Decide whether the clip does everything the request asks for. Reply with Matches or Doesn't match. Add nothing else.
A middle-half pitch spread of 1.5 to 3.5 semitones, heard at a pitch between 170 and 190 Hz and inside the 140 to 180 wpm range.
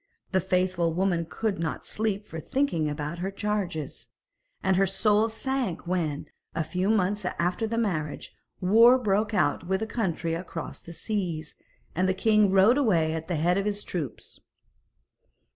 Doesn't match